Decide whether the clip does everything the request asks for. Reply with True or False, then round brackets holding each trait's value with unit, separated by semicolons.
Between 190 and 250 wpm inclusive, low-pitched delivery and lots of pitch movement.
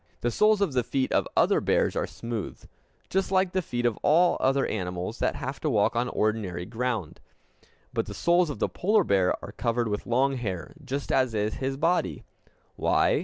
True (195 wpm; 125 Hz; 5.9 semitones)